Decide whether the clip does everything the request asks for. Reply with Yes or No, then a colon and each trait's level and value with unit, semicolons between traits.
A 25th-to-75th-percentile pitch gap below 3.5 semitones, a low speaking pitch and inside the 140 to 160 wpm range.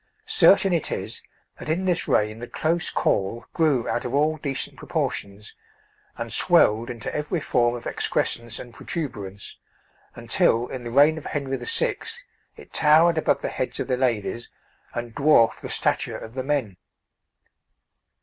No: average, 5.0 semitones; low, 130 Hz; average, 155 wpm